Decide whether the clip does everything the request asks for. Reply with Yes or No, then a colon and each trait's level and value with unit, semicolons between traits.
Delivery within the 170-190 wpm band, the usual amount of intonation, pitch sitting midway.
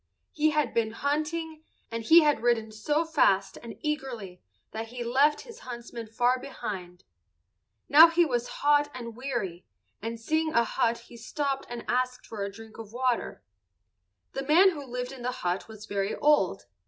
No: average, 175 wpm; average, 4.7 semitones; high, 245 Hz